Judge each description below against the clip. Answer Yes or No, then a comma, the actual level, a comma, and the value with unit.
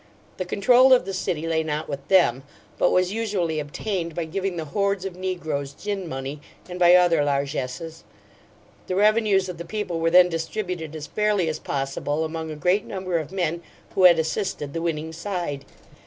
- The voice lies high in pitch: No, medium, 170 Hz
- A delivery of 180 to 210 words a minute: Yes, average, 185 wpm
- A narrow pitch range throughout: No, average, 3.4 semitones